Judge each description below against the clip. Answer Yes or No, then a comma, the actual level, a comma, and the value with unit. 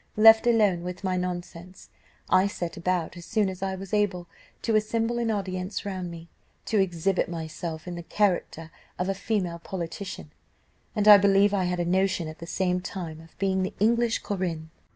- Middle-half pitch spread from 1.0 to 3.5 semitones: Yes, average, 2.7 semitones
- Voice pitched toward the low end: No, medium, 185 Hz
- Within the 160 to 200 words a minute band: Yes, average, 185 wpm